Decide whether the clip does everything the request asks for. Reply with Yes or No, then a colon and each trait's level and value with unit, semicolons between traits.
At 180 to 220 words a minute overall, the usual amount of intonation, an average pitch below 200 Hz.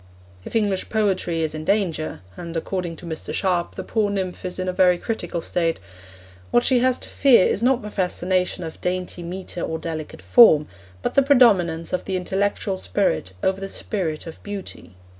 Yes: average, 185 wpm; average, 3.5 semitones; medium, 185 Hz